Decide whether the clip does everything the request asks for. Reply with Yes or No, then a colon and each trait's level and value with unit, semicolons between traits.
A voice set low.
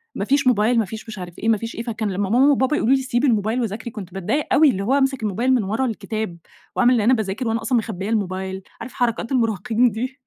No: high, 225 Hz